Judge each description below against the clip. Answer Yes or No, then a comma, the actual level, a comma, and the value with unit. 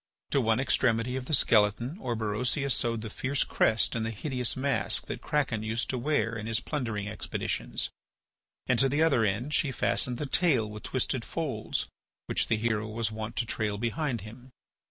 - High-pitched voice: No, low, 115 Hz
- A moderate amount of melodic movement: Yes, average, 3.2 semitones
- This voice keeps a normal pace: Yes, average, 180 wpm